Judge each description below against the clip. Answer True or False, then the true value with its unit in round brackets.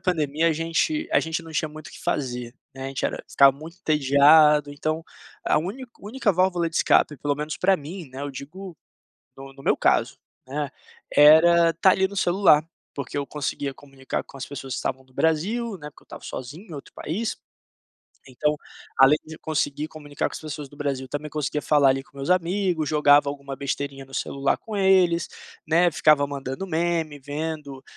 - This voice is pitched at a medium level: True (150 Hz)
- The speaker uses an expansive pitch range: False (3.2 semitones)